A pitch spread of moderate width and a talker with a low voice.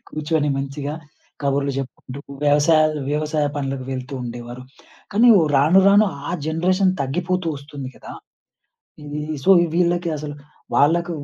No: average, 3.7 semitones; medium, 150 Hz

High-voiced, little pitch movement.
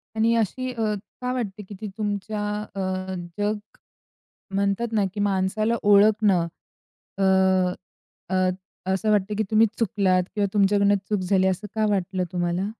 Yes: high, 205 Hz; narrow, 2.1 semitones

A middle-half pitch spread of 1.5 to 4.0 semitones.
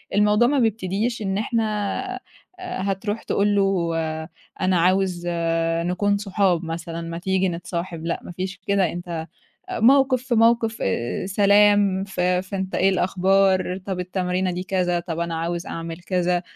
Yes: narrow, 2.5 semitones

